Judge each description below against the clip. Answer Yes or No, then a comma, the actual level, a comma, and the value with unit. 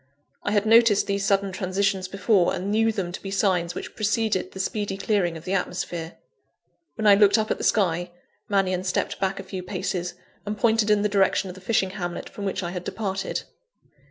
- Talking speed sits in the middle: No, fast, 210 wpm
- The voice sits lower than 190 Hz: No, high, 195 Hz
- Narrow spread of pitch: Yes, narrow, 2.2 semitones